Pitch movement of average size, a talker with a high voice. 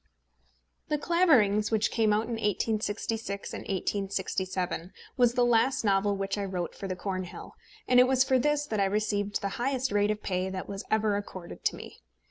Yes: average, 3.5 semitones; high, 210 Hz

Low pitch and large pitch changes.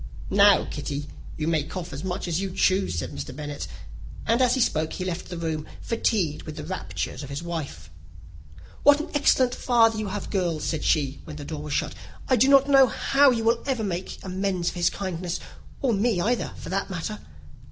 No: medium, 185 Hz; wide, 6.4 semitones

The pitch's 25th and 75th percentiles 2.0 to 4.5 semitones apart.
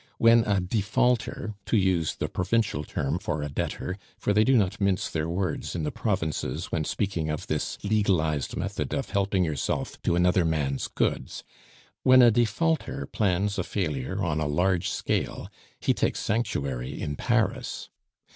No: average, 5.1 semitones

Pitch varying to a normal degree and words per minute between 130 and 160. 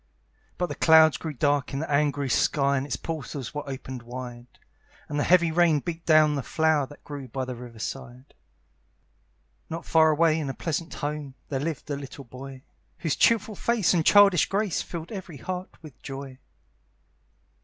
No: average, 3.4 semitones; average, 175 wpm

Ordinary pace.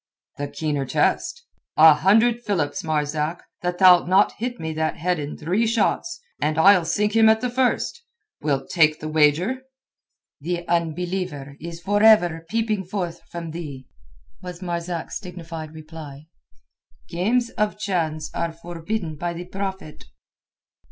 Yes: average, 145 wpm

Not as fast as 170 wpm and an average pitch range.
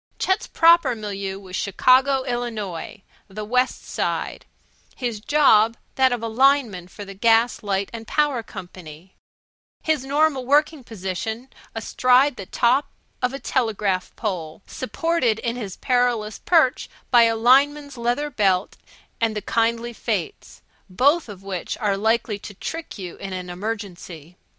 Yes: average, 140 wpm; average, 4.9 semitones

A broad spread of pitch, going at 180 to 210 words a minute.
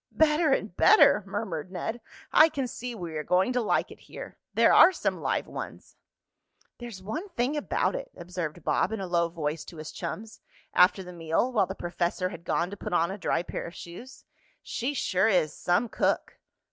Yes: wide, 5.9 semitones; average, 195 wpm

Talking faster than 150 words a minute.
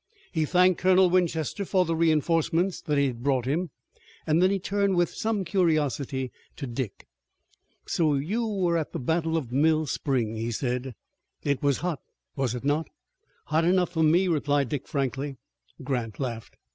Yes: average, 165 wpm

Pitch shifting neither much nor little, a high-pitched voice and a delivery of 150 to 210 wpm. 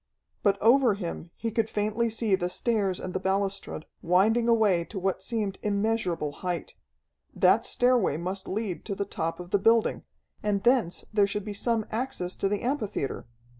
Yes: average, 3.2 semitones; high, 200 Hz; average, 170 wpm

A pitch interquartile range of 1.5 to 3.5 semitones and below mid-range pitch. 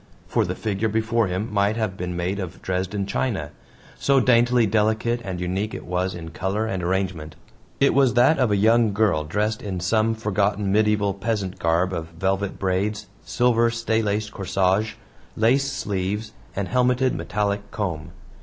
Yes: average, 3.1 semitones; low, 105 Hz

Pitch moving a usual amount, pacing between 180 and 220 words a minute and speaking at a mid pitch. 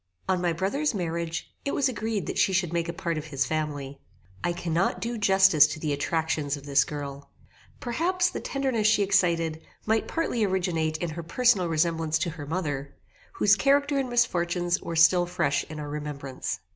Yes: average, 4.8 semitones; average, 185 wpm; medium, 170 Hz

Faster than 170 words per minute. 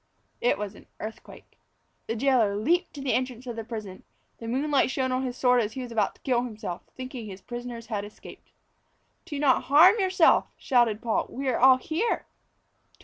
Yes: average, 190 wpm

